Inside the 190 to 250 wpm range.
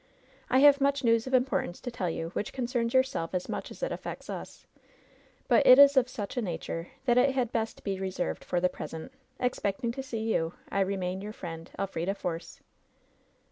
Yes: average, 200 wpm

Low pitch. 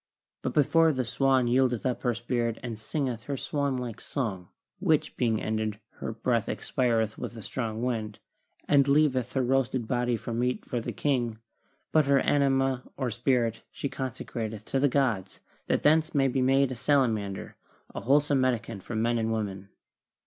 Yes: low, 125 Hz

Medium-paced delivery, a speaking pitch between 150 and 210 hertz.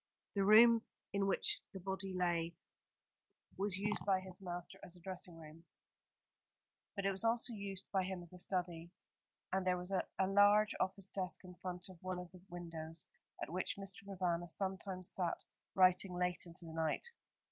Yes: average, 175 wpm; medium, 185 Hz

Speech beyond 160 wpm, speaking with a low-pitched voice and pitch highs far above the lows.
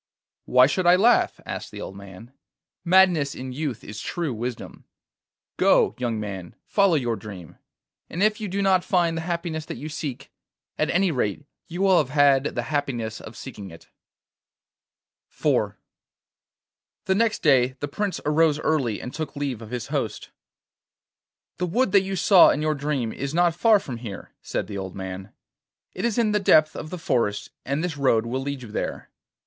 No: average, 180 wpm; medium, 145 Hz; wide, 6.9 semitones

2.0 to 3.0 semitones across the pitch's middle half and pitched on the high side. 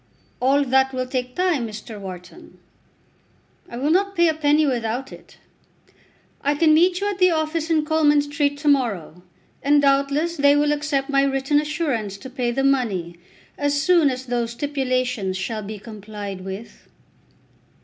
No: average, 4.2 semitones; very high, 275 Hz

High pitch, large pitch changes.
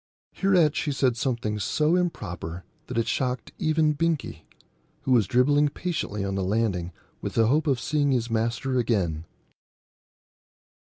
No: low, 125 Hz; wide, 5.9 semitones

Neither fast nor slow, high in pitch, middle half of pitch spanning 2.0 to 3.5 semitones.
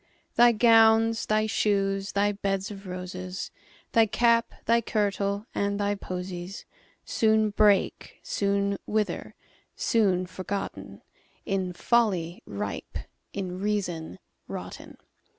No: slow, 90 wpm; high, 200 Hz; narrow, 2.6 semitones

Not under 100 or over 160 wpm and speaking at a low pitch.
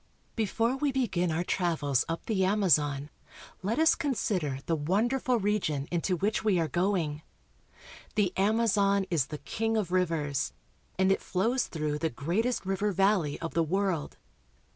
No: average, 150 wpm; high, 190 Hz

